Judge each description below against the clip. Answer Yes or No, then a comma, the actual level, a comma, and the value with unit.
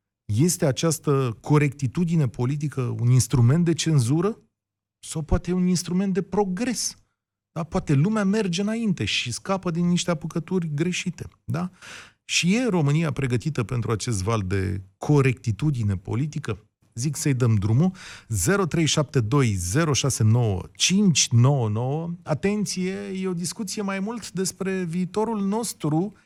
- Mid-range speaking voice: Yes, medium, 155 Hz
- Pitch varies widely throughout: Yes, wide, 7.1 semitones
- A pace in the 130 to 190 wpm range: No, slow, 115 wpm